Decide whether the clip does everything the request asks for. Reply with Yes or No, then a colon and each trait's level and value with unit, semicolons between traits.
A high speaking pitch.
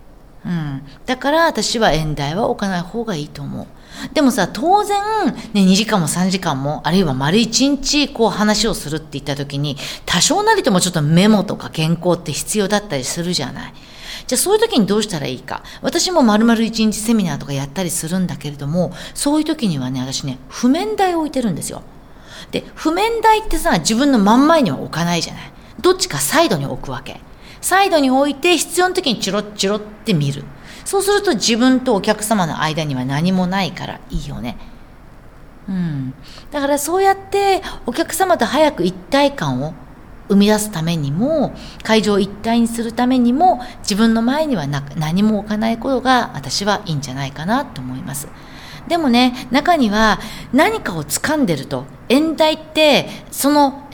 Yes: high, 220 Hz